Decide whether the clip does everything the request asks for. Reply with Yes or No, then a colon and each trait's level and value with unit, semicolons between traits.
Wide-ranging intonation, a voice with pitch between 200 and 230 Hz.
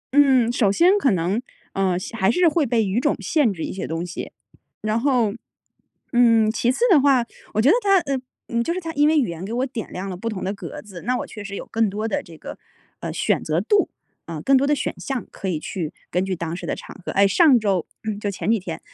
Yes: wide, 5.9 semitones; high, 225 Hz